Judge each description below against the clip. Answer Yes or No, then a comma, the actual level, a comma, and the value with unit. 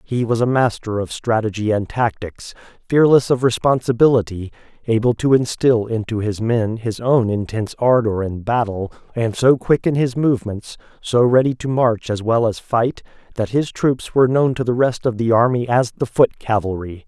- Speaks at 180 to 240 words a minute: Yes, average, 185 wpm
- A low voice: Yes, low, 115 Hz